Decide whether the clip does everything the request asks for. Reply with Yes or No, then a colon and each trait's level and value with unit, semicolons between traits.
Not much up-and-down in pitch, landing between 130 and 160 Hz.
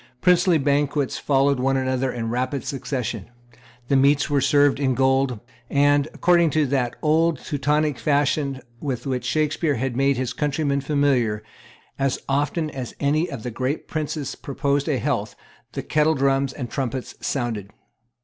Yes: narrow, 2.1 semitones; medium, 140 Hz